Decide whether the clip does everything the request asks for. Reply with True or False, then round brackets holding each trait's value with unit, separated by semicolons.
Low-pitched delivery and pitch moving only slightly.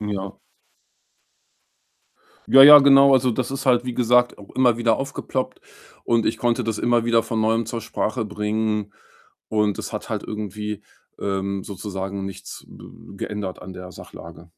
False (110 Hz; 3.5 semitones)